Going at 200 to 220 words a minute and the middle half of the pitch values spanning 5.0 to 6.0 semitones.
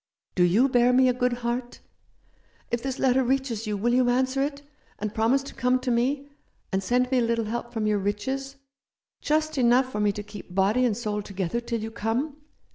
No: fast, 205 wpm; average, 3.4 semitones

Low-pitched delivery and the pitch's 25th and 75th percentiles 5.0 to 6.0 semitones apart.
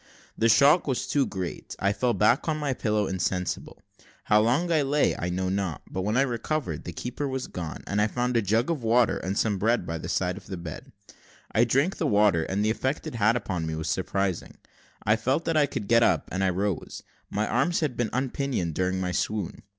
Yes: low, 110 Hz; wide, 5.5 semitones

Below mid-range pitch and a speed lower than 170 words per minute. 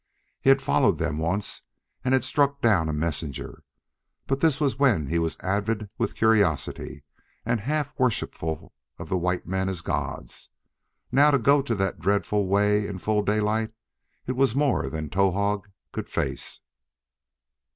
Yes: low, 105 Hz; average, 150 wpm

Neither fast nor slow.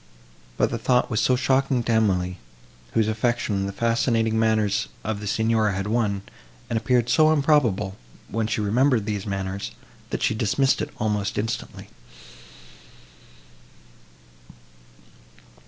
No: slow, 125 wpm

